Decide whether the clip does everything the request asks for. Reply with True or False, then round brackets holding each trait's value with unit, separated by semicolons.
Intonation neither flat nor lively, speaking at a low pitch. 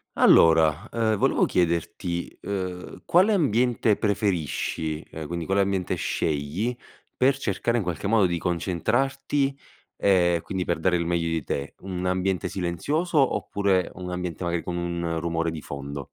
True (3.7 semitones; 90 Hz)